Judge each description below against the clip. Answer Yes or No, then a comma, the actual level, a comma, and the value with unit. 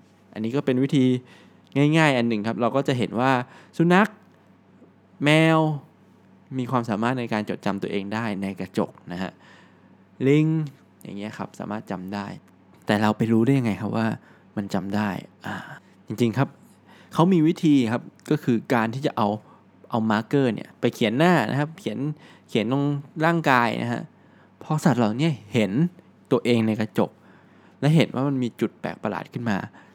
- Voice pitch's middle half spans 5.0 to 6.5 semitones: Yes, average, 5.3 semitones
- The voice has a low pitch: Yes, low, 125 Hz